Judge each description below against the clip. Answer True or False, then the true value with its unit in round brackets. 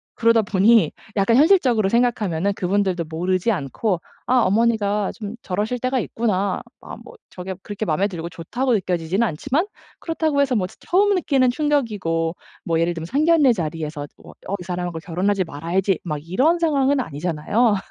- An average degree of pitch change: False (6.1 semitones)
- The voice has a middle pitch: False (205 Hz)